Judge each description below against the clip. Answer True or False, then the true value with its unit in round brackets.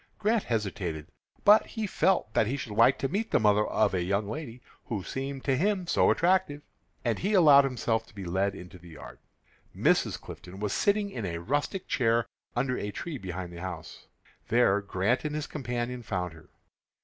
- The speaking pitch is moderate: False (115 Hz)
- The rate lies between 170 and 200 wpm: True (190 wpm)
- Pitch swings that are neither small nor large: False (7.1 semitones)